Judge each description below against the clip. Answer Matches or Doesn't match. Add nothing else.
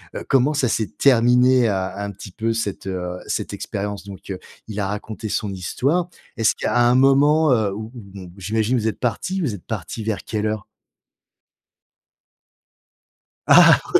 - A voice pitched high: Doesn't match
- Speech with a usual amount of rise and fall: Matches